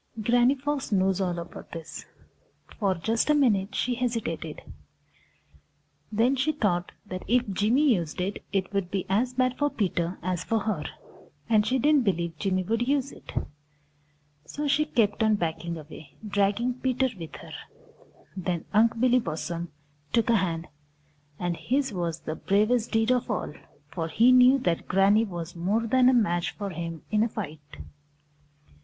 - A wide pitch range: Yes, wide, 5.9 semitones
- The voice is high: Yes, high, 210 Hz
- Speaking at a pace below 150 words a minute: No, average, 160 wpm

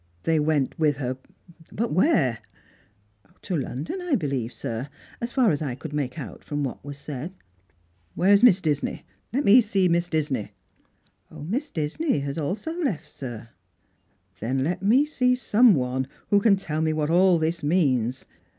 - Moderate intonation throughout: No, wide, 7.4 semitones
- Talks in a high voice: No, medium, 155 Hz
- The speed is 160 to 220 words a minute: Yes, average, 185 wpm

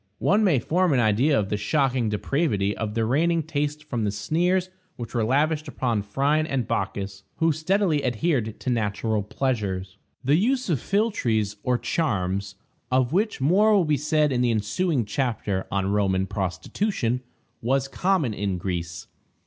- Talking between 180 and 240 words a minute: No, average, 160 wpm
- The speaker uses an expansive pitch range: Yes, wide, 7.0 semitones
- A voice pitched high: No, low, 125 Hz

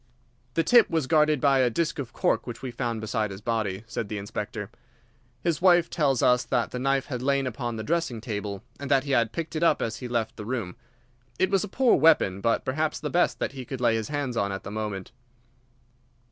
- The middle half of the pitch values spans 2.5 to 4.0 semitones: No, average, 5.3 semitones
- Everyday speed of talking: No, fast, 230 wpm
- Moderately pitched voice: No, low, 125 Hz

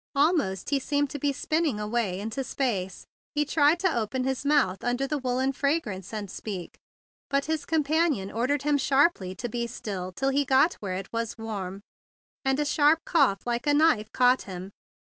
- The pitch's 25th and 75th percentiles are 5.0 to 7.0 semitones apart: Yes, wide, 5.6 semitones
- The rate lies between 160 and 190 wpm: Yes, average, 185 wpm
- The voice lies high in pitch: Yes, very high, 260 Hz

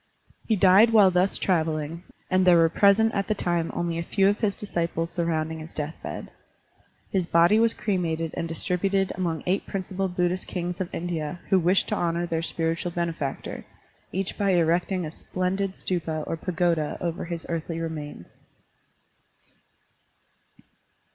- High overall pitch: No, medium, 175 Hz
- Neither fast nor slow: Yes, average, 155 wpm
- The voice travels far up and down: No, narrow, 2.5 semitones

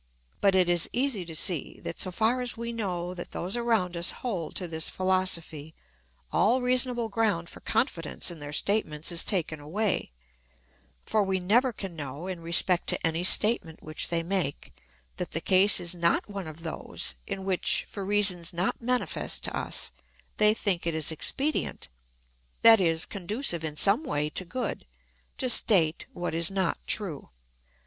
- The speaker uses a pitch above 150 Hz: Yes, medium, 185 Hz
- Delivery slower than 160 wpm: No, average, 170 wpm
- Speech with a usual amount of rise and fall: Yes, average, 4.4 semitones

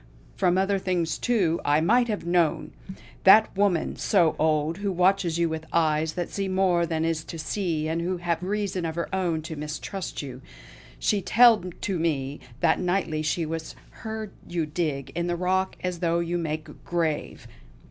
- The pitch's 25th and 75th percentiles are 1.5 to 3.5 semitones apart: Yes, average, 2.9 semitones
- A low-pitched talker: No, medium, 170 Hz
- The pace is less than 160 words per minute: No, average, 180 wpm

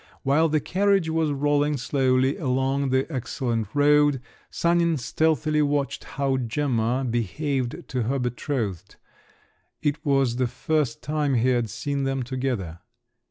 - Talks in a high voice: No, low, 135 Hz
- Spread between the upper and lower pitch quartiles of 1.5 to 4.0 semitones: Yes, average, 3.0 semitones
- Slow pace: Yes, slow, 130 wpm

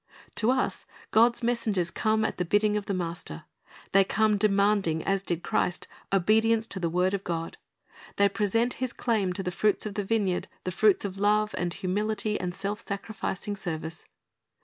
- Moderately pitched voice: No, high, 200 Hz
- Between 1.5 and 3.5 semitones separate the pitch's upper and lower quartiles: Yes, average, 2.9 semitones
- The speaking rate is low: No, average, 175 wpm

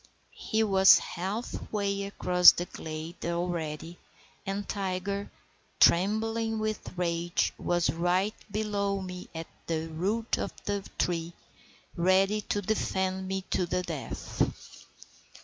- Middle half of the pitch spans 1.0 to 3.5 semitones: Yes, average, 2.8 semitones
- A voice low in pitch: No, high, 190 Hz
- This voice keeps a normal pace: No, slow, 115 wpm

